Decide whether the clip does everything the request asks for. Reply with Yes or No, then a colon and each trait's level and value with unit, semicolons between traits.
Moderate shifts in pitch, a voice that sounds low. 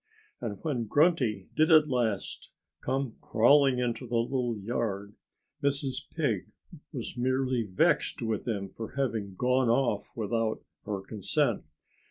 Yes: average, 3.6 semitones; low, 120 Hz